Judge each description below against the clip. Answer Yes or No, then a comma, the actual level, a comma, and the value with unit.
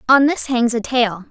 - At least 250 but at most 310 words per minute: No, fast, 230 wpm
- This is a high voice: Yes, high, 245 Hz